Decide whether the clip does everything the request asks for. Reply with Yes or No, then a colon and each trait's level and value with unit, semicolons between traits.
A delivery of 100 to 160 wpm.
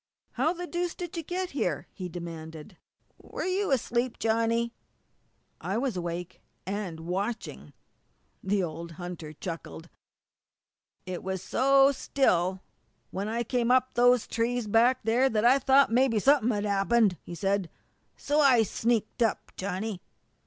Yes: average, 140 wpm